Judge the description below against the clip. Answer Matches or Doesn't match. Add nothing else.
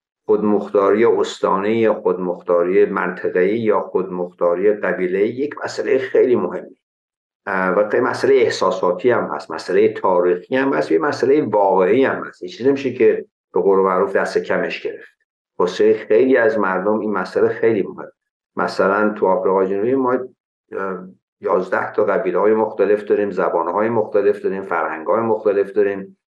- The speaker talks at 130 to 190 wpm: Matches